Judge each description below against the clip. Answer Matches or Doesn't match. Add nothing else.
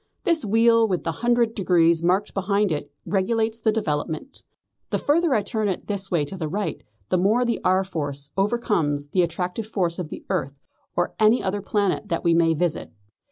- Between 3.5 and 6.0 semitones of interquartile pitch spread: Matches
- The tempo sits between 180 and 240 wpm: Matches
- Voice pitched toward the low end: Doesn't match